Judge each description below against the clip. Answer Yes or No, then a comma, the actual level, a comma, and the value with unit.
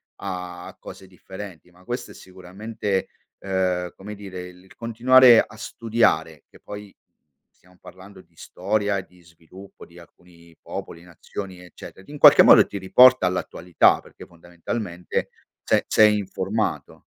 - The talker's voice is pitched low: Yes, very low, 95 Hz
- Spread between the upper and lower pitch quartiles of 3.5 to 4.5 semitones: No, narrow, 2.6 semitones